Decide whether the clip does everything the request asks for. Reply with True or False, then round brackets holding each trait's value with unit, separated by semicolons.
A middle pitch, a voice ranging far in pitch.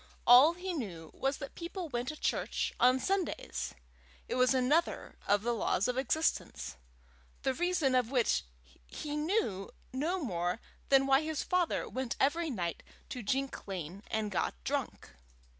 False (260 Hz; 6.3 semitones)